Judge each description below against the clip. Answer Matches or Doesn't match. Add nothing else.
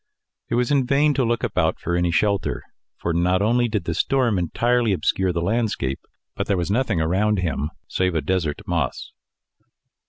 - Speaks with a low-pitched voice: Matches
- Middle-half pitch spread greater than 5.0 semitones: Matches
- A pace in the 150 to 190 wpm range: Matches